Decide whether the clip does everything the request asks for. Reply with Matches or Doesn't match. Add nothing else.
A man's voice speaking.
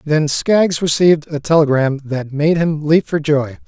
Matches